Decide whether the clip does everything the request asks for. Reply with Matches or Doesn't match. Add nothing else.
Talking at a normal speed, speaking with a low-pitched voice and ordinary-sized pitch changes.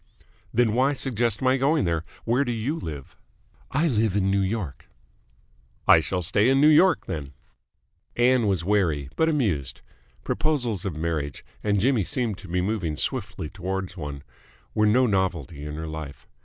Doesn't match